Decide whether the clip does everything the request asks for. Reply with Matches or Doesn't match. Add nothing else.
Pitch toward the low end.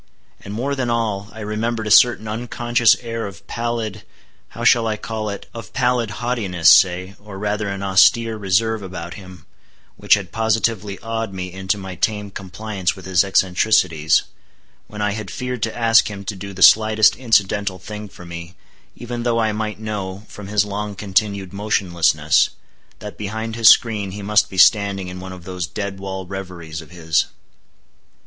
Matches